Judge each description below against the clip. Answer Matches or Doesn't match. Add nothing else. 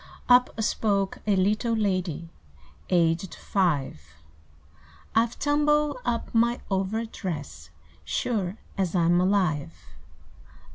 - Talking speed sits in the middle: Doesn't match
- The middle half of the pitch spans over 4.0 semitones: Matches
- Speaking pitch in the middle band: Doesn't match